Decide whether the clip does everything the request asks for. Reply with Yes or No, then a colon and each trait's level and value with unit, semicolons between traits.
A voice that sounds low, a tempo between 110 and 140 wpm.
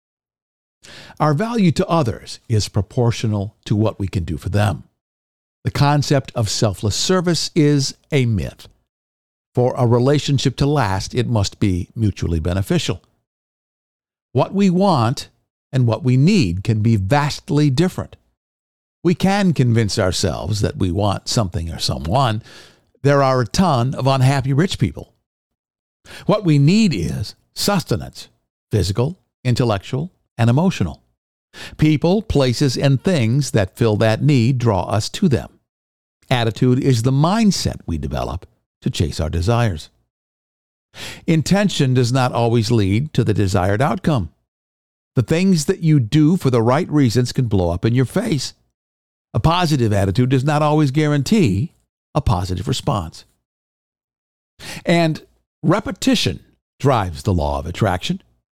Yes: low, 125 Hz; slow, 135 wpm